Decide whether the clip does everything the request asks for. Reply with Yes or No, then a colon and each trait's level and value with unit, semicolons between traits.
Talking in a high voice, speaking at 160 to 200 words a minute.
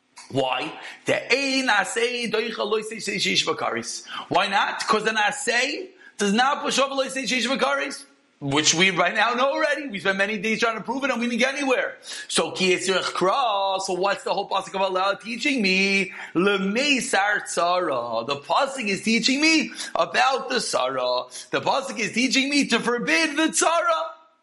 Yes: high, 230 Hz; average, 165 wpm